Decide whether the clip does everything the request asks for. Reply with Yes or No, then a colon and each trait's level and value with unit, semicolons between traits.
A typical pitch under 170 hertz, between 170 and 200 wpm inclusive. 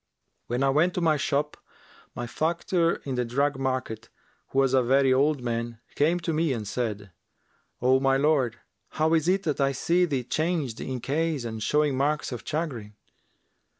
Yes: low, 135 Hz; average, 180 wpm